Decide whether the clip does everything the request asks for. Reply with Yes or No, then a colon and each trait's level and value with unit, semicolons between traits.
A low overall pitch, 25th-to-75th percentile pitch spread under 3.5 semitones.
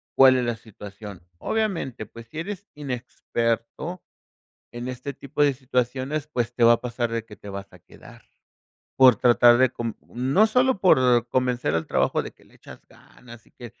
Yes: low, 125 Hz; average, 3.1 semitones